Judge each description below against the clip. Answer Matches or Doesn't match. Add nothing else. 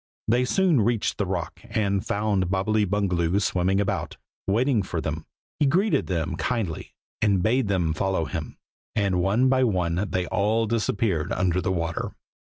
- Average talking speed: Matches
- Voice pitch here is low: Matches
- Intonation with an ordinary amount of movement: Matches